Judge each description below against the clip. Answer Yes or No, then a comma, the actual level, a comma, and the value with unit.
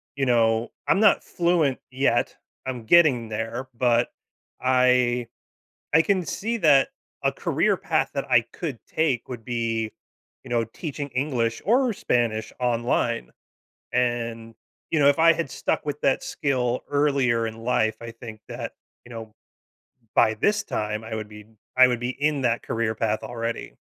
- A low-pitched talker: Yes, low, 120 Hz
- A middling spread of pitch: Yes, average, 3.7 semitones